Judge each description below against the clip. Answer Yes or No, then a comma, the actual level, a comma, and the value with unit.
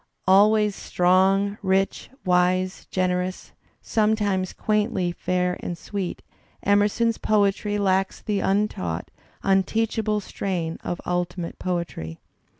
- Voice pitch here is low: No, high, 190 Hz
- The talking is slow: Yes, slow, 100 wpm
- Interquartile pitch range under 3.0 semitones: Yes, narrow, 2.4 semitones